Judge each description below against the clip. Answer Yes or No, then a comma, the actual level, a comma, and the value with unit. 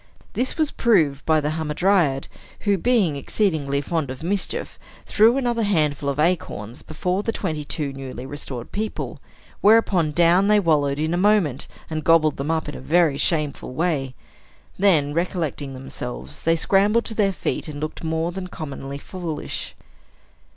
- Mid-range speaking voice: Yes, medium, 160 Hz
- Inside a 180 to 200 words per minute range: No, average, 160 wpm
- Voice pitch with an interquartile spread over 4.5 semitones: Yes, average, 5.2 semitones